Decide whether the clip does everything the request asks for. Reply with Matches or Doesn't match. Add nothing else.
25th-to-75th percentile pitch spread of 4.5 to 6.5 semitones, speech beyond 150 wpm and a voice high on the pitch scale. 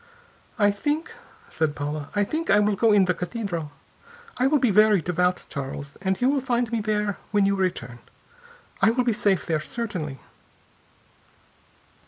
Matches